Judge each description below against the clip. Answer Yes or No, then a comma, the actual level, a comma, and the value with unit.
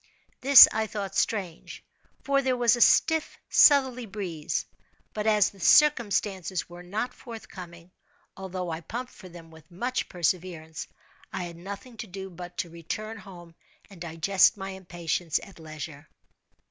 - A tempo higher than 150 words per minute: No, average, 145 wpm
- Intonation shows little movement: No, average, 4.4 semitones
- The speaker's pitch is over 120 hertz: Yes, high, 190 Hz